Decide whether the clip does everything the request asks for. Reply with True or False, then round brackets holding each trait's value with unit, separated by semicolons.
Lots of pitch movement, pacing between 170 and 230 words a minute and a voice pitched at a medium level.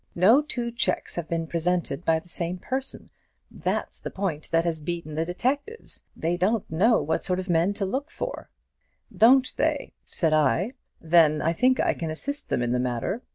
True (6.1 semitones; 190 wpm; 175 Hz)